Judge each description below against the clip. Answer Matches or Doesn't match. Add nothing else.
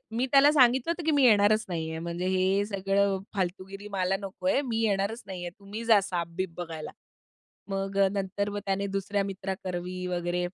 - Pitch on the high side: Matches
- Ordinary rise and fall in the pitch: Doesn't match